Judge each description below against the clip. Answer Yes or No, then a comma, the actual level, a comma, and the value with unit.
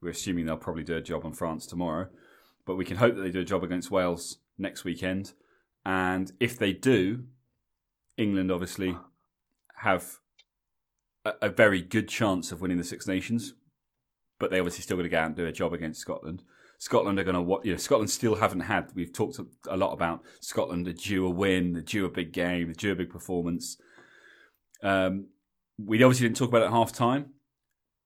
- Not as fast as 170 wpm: No, average, 200 wpm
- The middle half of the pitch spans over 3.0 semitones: No, average, 2.7 semitones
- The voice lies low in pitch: Yes, very low, 95 Hz